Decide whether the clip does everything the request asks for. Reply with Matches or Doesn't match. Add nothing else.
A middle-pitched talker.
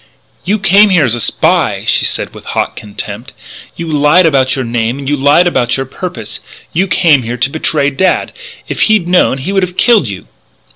Matches